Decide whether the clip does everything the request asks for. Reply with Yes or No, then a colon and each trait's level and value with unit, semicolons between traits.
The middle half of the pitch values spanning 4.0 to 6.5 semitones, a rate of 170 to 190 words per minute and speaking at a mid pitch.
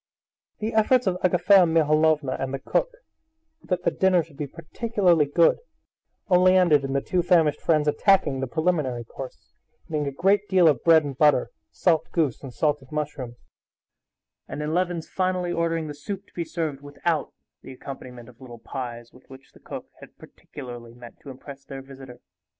Yes: average, 4.7 semitones; average, 175 wpm; medium, 150 Hz